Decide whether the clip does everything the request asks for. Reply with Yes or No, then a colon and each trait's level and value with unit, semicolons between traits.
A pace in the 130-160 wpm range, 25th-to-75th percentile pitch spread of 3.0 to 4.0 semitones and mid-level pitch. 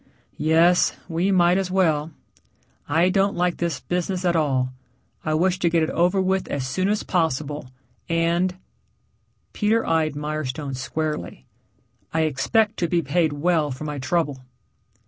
Yes: average, 150 wpm; average, 3.3 semitones; medium, 165 Hz